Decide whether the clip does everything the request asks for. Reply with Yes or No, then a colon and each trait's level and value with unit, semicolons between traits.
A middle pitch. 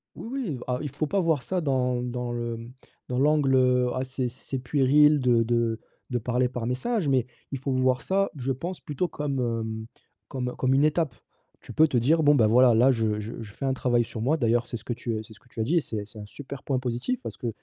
No: low, 125 Hz